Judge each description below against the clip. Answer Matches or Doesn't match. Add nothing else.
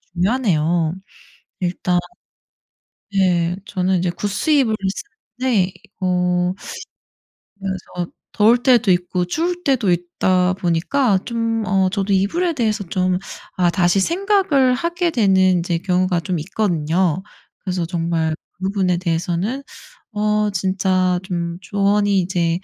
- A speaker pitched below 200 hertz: Matches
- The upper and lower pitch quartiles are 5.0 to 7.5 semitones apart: Doesn't match